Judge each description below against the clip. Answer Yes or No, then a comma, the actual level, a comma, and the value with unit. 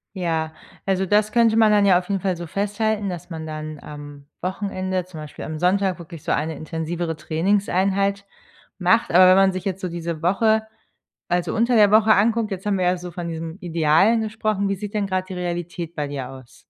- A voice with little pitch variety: No, average, 3.5 semitones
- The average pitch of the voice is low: No, medium, 185 Hz